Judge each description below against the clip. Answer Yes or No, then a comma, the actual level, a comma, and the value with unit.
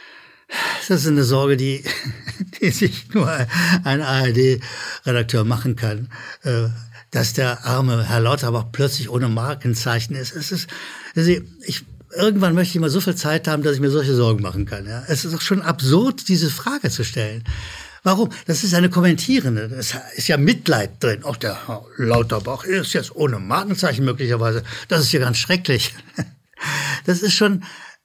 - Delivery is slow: No, average, 165 wpm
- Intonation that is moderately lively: No, wide, 6.6 semitones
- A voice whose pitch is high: No, low, 135 Hz